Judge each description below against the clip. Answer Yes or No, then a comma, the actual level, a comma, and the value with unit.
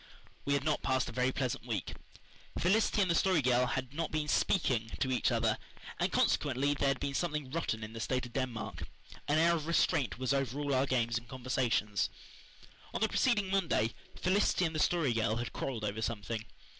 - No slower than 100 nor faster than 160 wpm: No, average, 200 wpm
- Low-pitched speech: Yes, low, 130 Hz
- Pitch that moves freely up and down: No, average, 4.9 semitones